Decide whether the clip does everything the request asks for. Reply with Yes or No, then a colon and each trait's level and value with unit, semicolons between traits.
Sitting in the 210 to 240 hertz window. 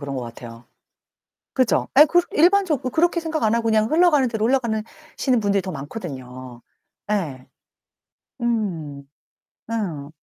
Yes: high, 215 Hz